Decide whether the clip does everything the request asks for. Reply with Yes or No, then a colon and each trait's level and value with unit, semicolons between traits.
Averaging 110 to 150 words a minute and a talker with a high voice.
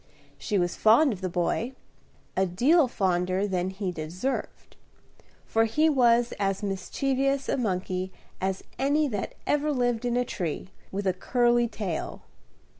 Yes: average, 145 wpm; high, 215 Hz